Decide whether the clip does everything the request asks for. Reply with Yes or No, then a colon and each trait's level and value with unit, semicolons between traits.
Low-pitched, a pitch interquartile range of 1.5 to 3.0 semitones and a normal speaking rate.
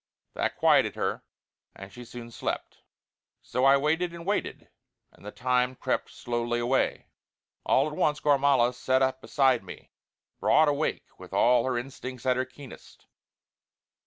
Yes: low, 130 Hz; average, 2.7 semitones; average, 155 wpm